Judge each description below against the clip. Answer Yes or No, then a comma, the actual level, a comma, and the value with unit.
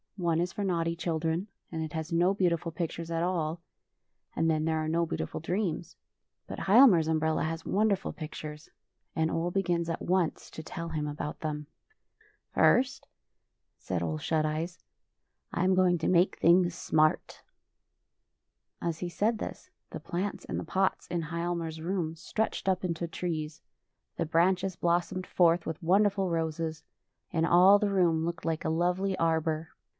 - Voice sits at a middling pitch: Yes, medium, 170 Hz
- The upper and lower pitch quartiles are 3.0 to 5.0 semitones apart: No, narrow, 2.4 semitones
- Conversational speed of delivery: Yes, average, 170 wpm